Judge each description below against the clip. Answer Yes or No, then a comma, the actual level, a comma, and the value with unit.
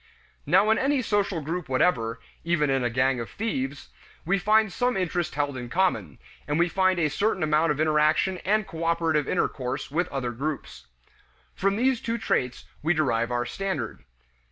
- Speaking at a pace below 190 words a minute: Yes, average, 170 wpm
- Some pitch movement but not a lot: No, wide, 6.1 semitones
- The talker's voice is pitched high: No, medium, 160 Hz